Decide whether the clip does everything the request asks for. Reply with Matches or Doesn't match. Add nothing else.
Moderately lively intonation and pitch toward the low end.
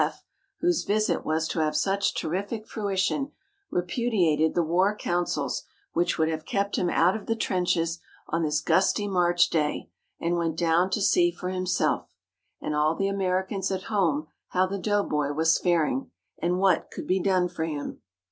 Doesn't match